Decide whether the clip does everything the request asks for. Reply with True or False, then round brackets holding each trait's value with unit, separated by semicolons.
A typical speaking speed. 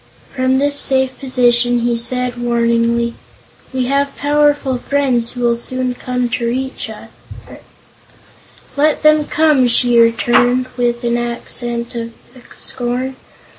False (125 wpm)